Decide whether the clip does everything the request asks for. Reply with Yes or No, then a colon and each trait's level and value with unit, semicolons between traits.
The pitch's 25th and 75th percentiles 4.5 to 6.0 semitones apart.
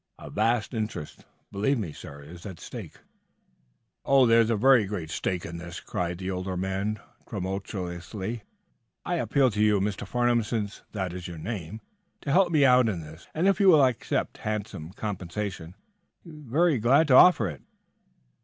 Yes: wide, 5.4 semitones